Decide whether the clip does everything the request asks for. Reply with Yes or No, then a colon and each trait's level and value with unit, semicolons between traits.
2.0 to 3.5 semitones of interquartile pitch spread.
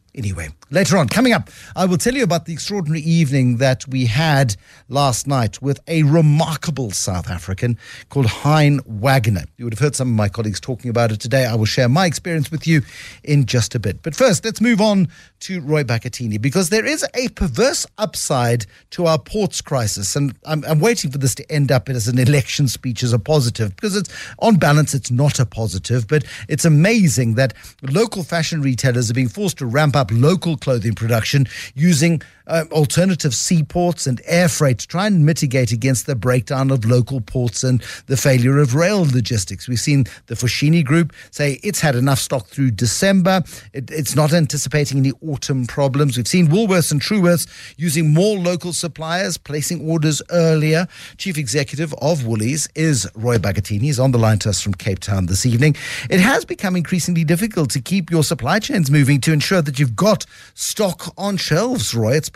No: average, 5.2 semitones